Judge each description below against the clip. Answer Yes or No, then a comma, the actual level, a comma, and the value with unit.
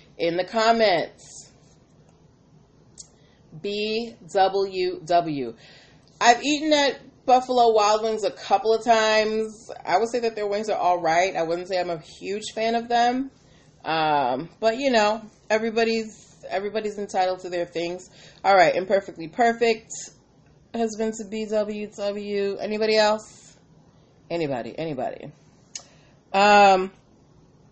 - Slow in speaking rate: Yes, slow, 130 wpm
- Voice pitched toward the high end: Yes, high, 205 Hz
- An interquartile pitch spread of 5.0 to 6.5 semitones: No, average, 4.6 semitones